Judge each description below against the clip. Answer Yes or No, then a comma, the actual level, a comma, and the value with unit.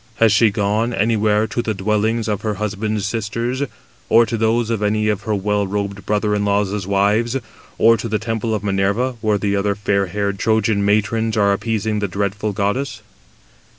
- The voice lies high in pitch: No, low, 105 Hz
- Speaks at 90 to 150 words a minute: No, average, 185 wpm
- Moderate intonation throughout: No, narrow, 1.8 semitones